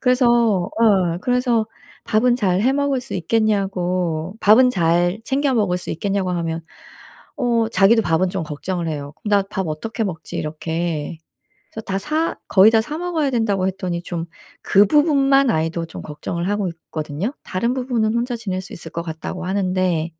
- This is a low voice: No, high, 195 Hz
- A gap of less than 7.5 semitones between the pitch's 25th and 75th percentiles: Yes, wide, 5.5 semitones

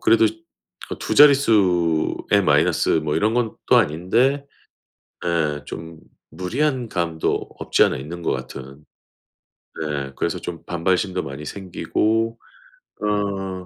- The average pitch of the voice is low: Yes, very low, 90 Hz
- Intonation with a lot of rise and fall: Yes, wide, 5.7 semitones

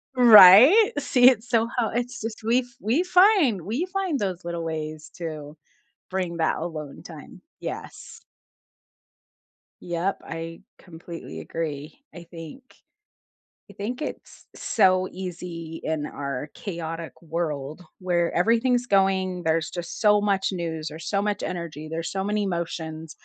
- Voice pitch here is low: No, medium, 180 Hz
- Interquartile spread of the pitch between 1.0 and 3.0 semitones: No, average, 5.1 semitones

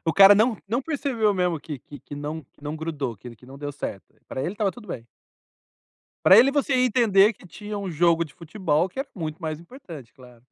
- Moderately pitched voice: Yes, medium, 170 Hz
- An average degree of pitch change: No, wide, 6.4 semitones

